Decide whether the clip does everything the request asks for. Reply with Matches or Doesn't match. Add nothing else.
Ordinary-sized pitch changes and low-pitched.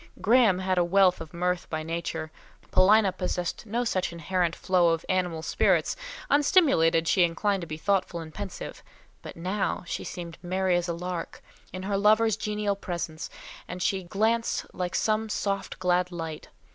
Doesn't match